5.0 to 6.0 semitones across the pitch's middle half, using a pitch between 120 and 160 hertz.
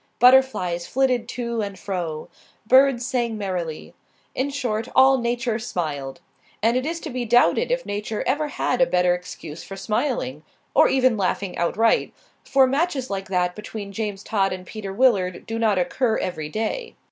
No: wide, 5.6 semitones; high, 220 Hz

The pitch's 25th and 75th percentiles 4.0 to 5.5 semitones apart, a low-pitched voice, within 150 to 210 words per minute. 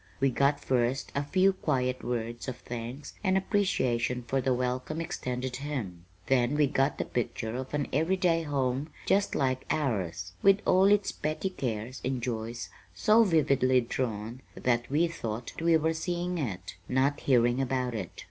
Yes: average, 4.4 semitones; low, 130 Hz; average, 160 wpm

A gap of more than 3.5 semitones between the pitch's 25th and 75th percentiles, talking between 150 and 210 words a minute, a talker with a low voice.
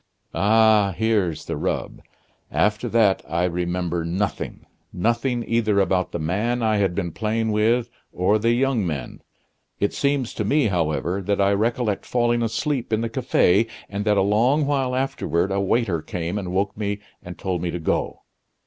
Yes: average, 4.2 semitones; average, 170 wpm; low, 105 Hz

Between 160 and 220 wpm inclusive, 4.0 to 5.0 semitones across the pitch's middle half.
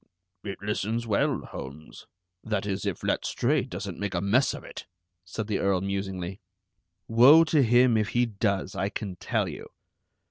No: average, 165 wpm; average, 3.1 semitones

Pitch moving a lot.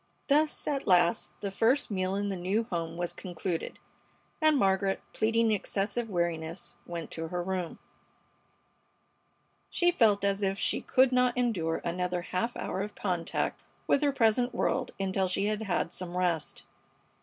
No: average, 4.3 semitones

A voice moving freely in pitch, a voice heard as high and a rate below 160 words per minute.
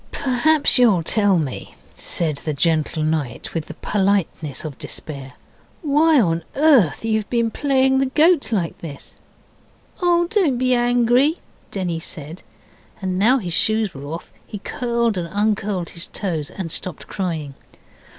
Yes: wide, 7.3 semitones; high, 200 Hz; average, 140 wpm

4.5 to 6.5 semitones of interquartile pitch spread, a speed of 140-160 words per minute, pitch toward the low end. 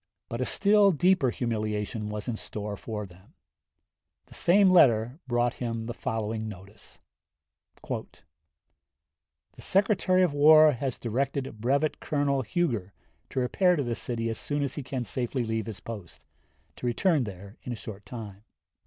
Yes: average, 5.0 semitones; average, 155 wpm; low, 120 Hz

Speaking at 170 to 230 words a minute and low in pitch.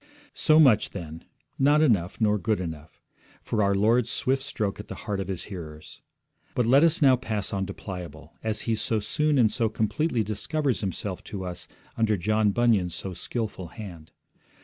Yes: average, 180 wpm; low, 105 Hz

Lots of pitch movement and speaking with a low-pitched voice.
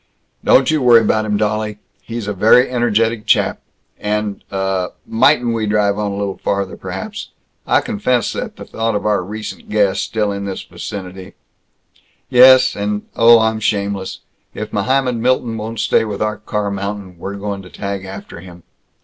No: narrow, 2.4 semitones; low, 105 Hz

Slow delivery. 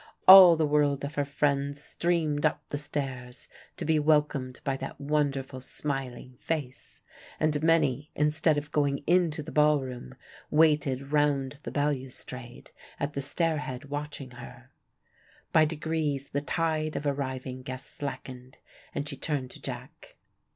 No: average, 150 wpm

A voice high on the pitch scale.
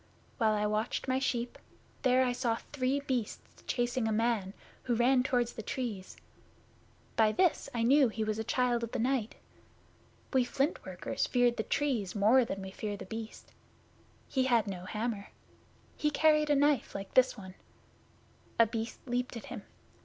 Yes: high, 240 Hz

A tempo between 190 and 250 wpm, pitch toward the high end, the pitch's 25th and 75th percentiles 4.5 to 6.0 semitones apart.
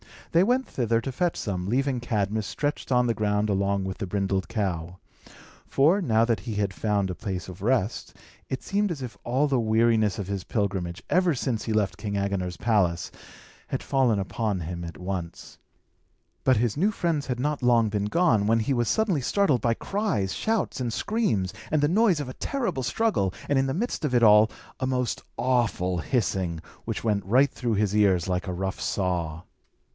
No: average, 195 wpm; low, 110 Hz; wide, 5.5 semitones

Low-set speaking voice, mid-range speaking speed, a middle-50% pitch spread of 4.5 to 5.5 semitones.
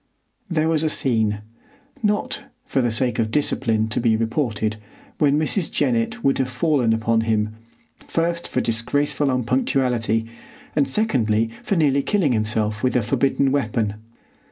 Yes: low, 125 Hz; average, 145 wpm; average, 4.9 semitones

